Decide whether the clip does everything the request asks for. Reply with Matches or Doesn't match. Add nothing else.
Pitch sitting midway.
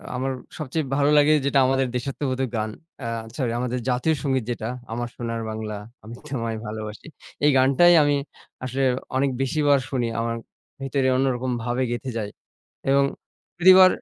Doesn't match